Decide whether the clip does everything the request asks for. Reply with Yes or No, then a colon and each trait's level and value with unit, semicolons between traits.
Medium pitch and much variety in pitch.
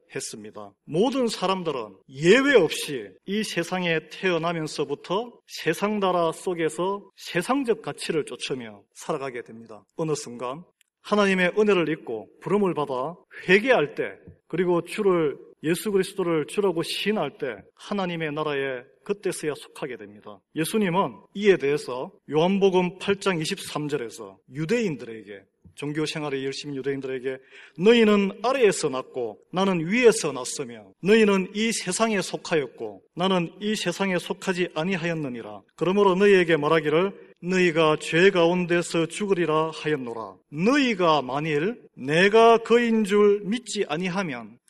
No: medium, 175 Hz; average, 4.8 semitones